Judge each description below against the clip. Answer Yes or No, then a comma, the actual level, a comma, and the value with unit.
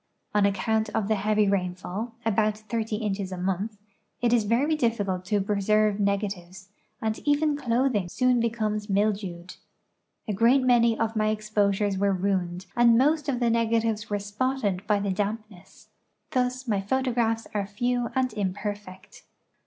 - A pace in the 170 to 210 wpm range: No, average, 155 wpm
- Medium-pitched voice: No, high, 215 Hz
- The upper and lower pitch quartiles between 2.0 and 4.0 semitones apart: Yes, average, 2.8 semitones